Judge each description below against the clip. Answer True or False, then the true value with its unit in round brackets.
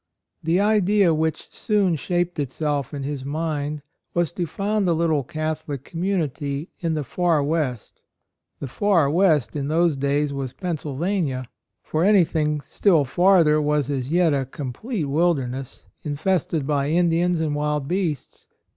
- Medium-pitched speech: True (155 Hz)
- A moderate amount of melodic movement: True (3.5 semitones)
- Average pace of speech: True (145 wpm)